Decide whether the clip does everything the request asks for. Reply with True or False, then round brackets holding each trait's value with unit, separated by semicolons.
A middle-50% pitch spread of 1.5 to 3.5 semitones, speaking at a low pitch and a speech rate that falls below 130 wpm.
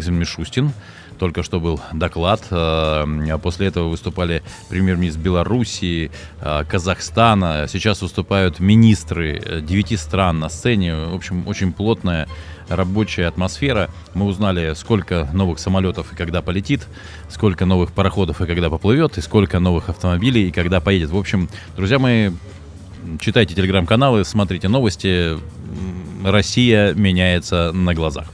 True (2.9 semitones; 90 Hz; 120 wpm)